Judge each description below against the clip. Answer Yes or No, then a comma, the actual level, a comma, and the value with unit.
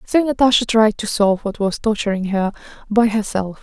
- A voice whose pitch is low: No, high, 215 Hz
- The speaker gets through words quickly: No, average, 180 wpm